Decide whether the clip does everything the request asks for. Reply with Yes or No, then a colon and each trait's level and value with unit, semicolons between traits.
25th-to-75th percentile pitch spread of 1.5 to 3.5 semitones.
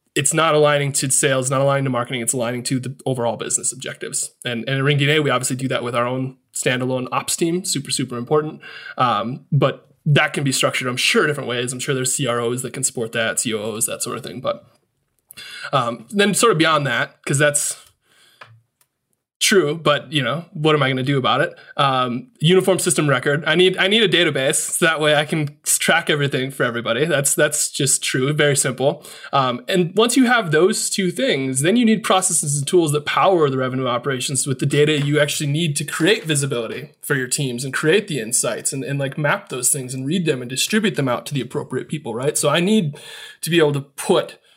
Yes: average, 3.2 semitones